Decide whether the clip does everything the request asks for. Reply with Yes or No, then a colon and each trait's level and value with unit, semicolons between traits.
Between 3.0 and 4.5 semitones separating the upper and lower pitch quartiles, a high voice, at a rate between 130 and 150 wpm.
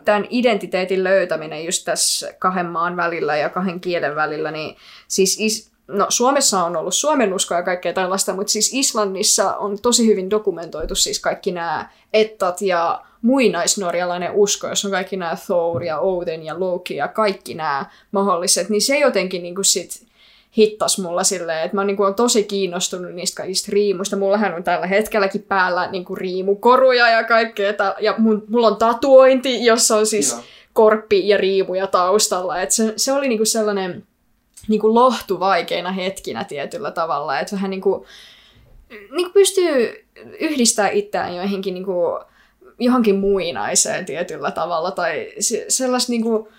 Yes: average, 3.3 semitones; high, 200 Hz; average, 140 wpm